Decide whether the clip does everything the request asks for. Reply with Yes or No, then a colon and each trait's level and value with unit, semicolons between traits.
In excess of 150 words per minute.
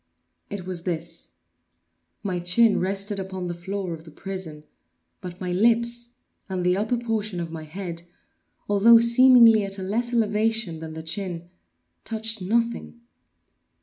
No: average, 145 wpm